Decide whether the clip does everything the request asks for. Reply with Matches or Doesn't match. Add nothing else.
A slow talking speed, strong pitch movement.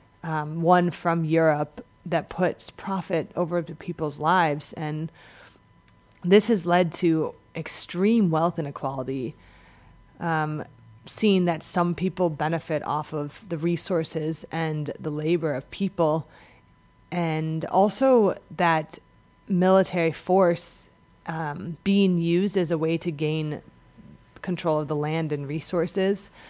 Doesn't match